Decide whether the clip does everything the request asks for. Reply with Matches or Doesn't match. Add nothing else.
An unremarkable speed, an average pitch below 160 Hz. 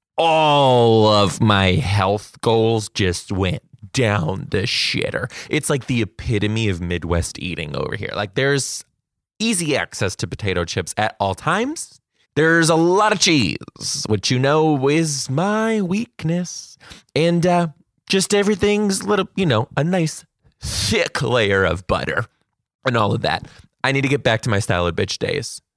Matches